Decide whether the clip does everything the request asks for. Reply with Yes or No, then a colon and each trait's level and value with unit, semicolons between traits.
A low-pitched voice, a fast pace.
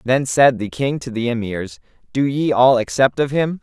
Yes: low, 125 Hz; fast, 215 wpm